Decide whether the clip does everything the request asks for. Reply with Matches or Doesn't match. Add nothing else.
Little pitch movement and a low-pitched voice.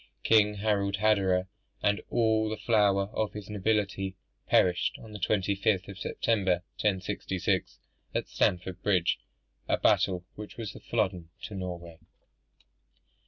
Matches